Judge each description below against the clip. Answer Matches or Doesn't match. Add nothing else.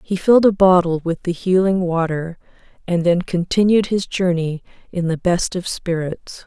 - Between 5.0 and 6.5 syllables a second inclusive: Doesn't match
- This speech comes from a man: Doesn't match